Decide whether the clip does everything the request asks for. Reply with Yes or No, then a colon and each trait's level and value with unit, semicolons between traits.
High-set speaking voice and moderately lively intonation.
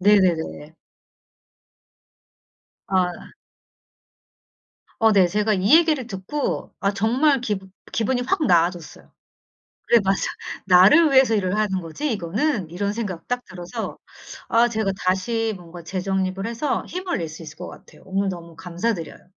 Yes: high, 195 Hz; average, 4.4 semitones